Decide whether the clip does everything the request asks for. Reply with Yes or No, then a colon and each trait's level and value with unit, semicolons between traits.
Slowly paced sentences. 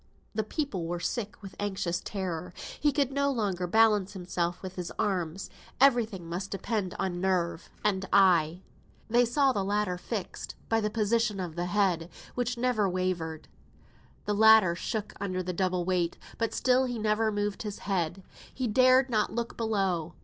No: average, 170 wpm